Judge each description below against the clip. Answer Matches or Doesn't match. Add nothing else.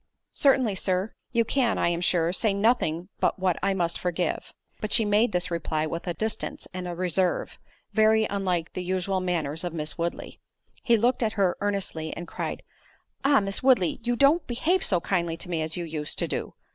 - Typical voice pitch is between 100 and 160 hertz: Doesn't match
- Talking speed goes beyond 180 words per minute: Matches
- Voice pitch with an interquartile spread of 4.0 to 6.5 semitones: Matches